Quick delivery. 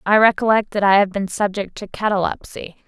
No: average, 190 wpm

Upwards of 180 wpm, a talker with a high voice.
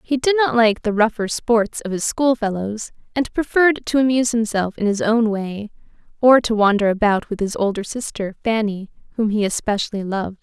Yes: average, 190 wpm; high, 220 Hz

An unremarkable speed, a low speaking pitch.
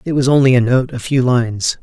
No: fast, 265 wpm; low, 125 Hz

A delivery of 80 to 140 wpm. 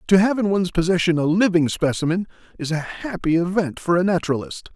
No: average, 190 wpm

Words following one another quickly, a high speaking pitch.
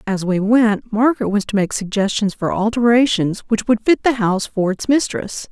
No: average, 195 wpm; high, 215 Hz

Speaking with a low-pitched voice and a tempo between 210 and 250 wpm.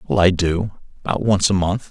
Yes: very low, 95 Hz; fast, 220 wpm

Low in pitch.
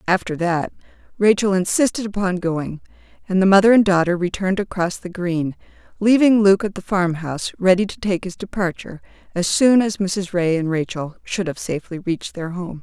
No: medium, 185 Hz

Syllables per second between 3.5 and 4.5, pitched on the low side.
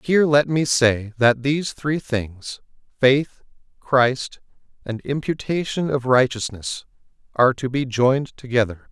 Yes: 4.3 syllables/s; low, 130 Hz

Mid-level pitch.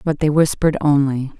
Yes: medium, 145 Hz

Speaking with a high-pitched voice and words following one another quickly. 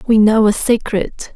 No: high, 220 Hz; average, 175 wpm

